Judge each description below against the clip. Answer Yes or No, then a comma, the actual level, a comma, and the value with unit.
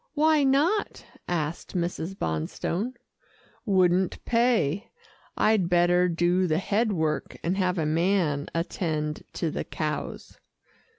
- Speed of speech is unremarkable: No, slow, 115 wpm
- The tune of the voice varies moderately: Yes, average, 4.1 semitones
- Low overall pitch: No, medium, 180 Hz